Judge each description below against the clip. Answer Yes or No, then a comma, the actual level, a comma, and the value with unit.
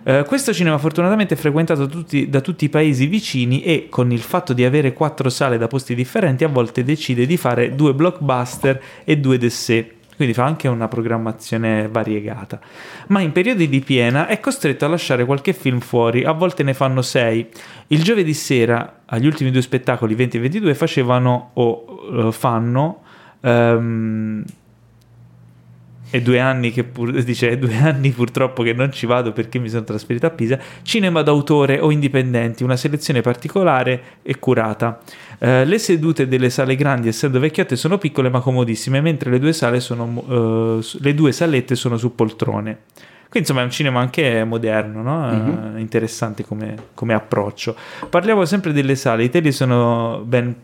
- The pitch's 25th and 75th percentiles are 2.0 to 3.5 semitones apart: No, average, 4.2 semitones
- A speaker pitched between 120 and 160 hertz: Yes, low, 125 Hz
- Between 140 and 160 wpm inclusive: No, fast, 170 wpm